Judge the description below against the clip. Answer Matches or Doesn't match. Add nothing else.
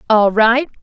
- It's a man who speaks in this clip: Doesn't match